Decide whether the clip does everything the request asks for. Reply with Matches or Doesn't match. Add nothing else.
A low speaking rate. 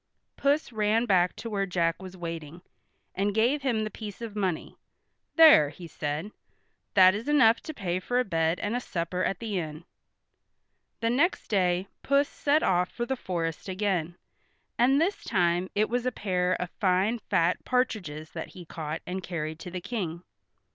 Doesn't match